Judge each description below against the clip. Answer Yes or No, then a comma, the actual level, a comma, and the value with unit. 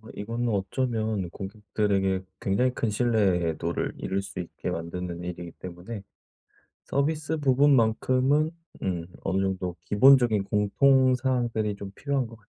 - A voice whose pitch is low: Yes, low, 105 Hz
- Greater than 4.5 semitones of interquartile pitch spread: Yes, average, 5.1 semitones